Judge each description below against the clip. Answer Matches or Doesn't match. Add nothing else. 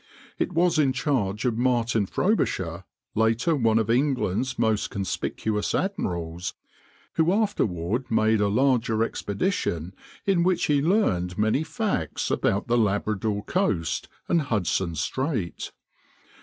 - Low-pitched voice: Matches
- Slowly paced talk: Matches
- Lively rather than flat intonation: Matches